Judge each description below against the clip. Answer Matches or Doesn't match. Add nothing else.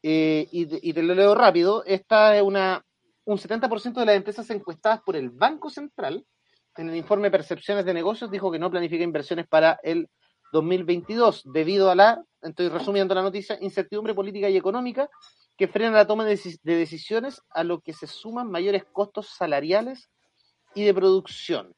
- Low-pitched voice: Doesn't match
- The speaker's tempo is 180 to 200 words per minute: Doesn't match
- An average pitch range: Matches